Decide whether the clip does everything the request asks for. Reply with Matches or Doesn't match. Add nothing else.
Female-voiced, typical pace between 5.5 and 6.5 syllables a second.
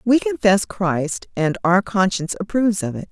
Doesn't match